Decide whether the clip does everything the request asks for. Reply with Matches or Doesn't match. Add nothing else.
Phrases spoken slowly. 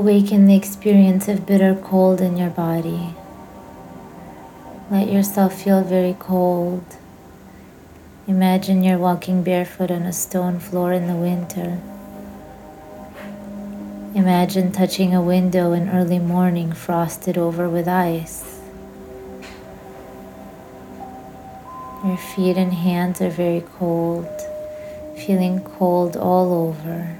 Matches